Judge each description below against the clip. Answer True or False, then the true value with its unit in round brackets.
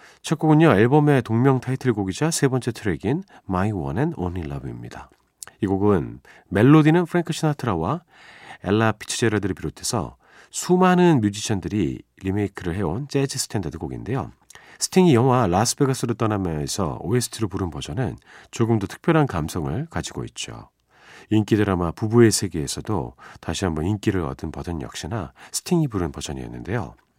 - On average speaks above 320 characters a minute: True (375 characters per minute)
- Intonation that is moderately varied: False (6.8 semitones)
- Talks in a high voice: False (110 Hz)